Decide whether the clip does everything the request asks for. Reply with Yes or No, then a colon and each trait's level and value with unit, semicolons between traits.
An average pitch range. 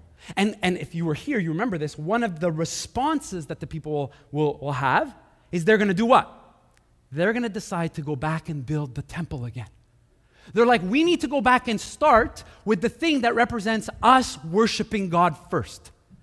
No: wide, 7.2 semitones